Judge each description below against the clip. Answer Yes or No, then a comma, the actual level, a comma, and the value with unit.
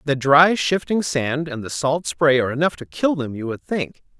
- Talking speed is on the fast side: Yes, fast, 230 wpm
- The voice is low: No, medium, 150 Hz